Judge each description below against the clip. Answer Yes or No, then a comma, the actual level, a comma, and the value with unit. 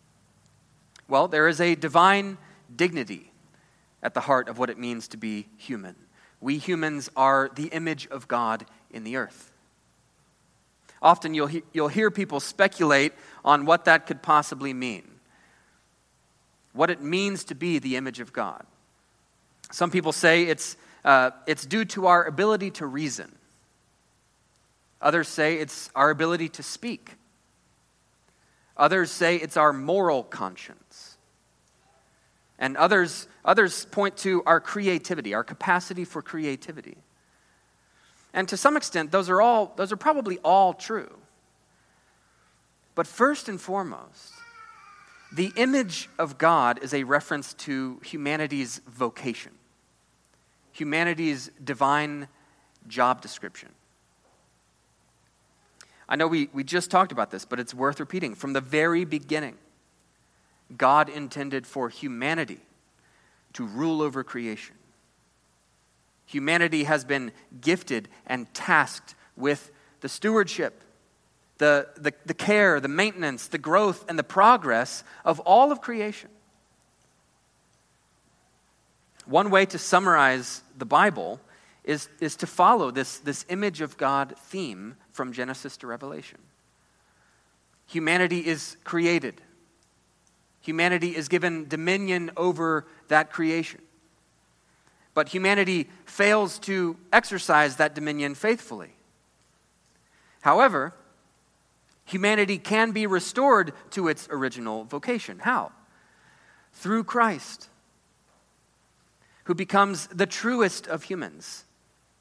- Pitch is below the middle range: No, medium, 160 Hz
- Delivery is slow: Yes, slow, 115 wpm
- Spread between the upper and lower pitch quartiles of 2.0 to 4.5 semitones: No, average, 5.0 semitones